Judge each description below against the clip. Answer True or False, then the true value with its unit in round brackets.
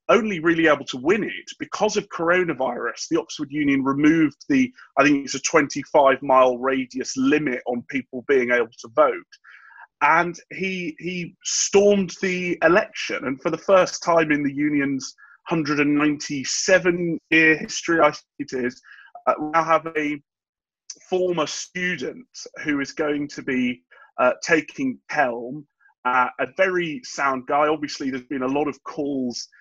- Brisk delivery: False (150 wpm)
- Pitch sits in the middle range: True (155 Hz)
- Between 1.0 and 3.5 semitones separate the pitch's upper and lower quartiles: False (5.0 semitones)